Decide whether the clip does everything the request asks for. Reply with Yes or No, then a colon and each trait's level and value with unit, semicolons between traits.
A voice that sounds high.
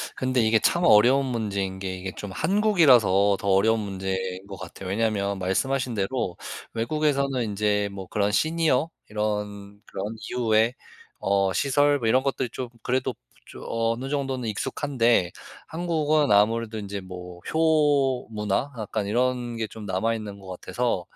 No: low, 110 Hz